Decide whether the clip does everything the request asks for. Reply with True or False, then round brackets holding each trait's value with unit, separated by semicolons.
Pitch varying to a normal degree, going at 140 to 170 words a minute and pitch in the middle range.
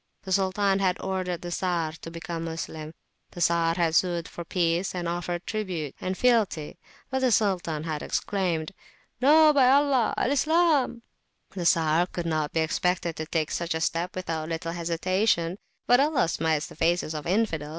False (3.3 semitones; 185 wpm; 175 Hz)